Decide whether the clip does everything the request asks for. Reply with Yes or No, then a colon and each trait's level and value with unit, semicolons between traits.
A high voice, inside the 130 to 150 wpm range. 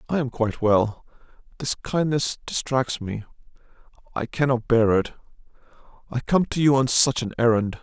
No: low, 125 Hz; average, 140 wpm